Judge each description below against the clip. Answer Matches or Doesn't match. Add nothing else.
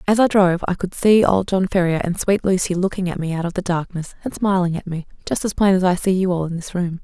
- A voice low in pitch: Doesn't match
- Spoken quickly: Matches